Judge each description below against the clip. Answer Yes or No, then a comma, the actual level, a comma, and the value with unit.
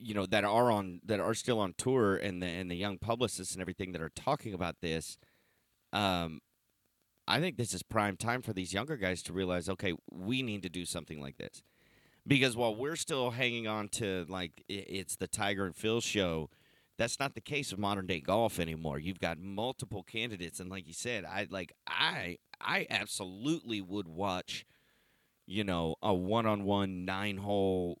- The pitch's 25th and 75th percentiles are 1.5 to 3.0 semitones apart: No, average, 3.4 semitones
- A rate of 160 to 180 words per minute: No, average, 195 wpm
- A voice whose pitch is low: Yes, low, 100 Hz